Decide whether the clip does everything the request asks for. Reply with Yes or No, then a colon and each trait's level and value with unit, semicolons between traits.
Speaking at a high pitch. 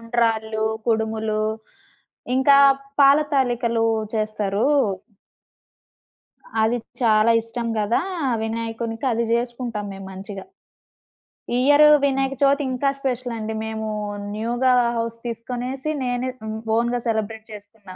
Yes: high, 230 Hz